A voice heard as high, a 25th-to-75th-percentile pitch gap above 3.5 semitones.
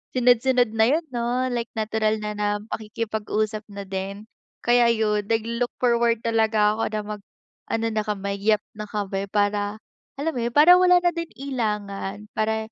No: high, 220 Hz; narrow, 2.4 semitones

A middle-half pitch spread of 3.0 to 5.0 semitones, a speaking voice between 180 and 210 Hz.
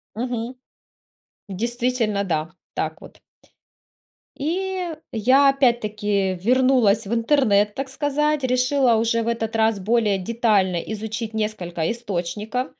No: average, 3.6 semitones; high, 230 Hz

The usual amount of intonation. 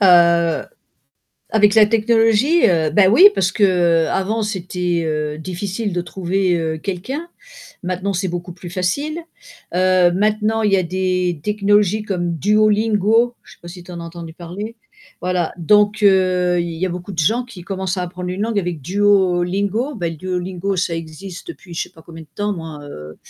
Yes: average, 3.2 semitones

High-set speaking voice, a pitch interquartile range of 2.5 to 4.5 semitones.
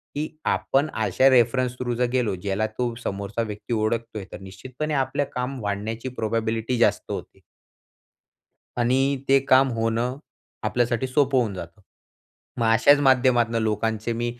No: low, 120 Hz; average, 2.9 semitones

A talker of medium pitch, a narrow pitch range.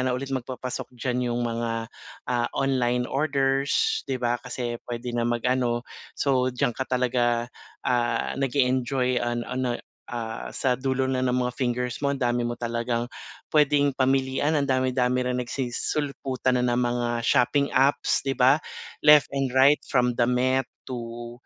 No: low, 125 Hz; narrow, 1.7 semitones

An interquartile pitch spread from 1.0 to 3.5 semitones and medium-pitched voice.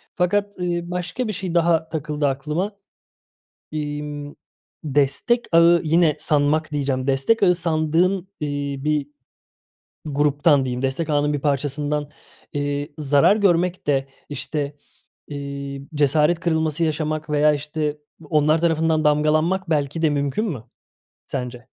Yes: narrow, 2.6 semitones; medium, 150 Hz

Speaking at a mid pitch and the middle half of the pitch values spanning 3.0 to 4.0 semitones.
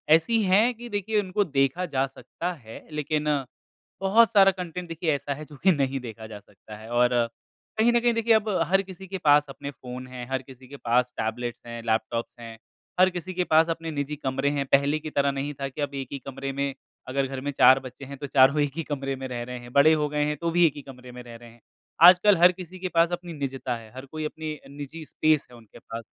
No: medium, 145 Hz; average, 5.0 semitones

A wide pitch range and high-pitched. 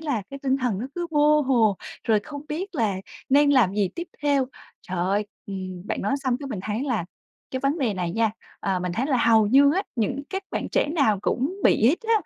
Yes: wide, 5.7 semitones; very high, 255 Hz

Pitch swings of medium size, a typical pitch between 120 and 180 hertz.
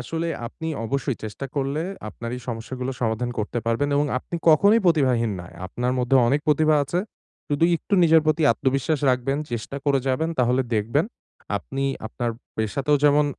Yes: average, 3.9 semitones; low, 135 Hz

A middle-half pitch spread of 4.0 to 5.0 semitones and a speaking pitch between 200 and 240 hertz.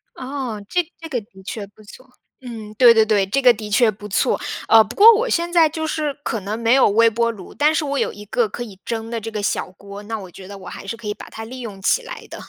Yes: average, 4.6 semitones; high, 225 Hz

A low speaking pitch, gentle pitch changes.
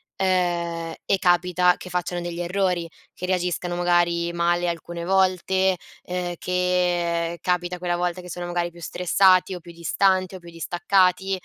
No: medium, 175 Hz; narrow, 1.0 semitones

